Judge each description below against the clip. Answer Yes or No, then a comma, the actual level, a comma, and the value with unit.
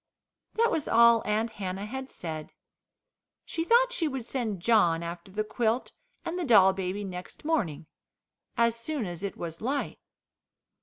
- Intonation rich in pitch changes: Yes, wide, 6.2 semitones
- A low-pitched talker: No, high, 220 Hz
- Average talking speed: Yes, average, 155 wpm